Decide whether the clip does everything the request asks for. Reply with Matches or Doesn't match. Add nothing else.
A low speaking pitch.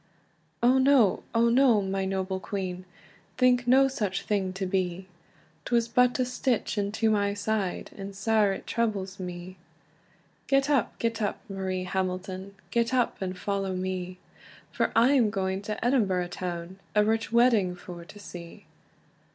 Doesn't match